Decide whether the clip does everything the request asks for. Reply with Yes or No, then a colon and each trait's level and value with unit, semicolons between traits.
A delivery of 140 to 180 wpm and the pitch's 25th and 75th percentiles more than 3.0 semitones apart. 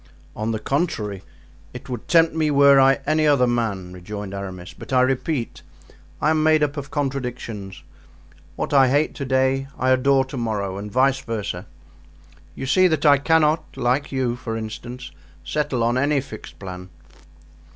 Yes: average, 165 wpm; average, 4.5 semitones